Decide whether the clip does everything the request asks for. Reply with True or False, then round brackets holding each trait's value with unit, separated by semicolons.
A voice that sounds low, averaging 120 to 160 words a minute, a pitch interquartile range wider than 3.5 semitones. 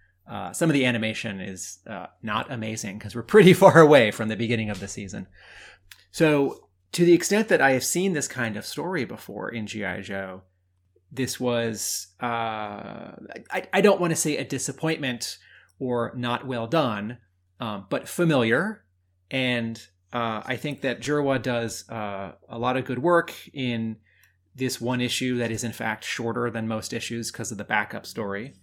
False (120 Hz; 175 wpm; 4.6 semitones)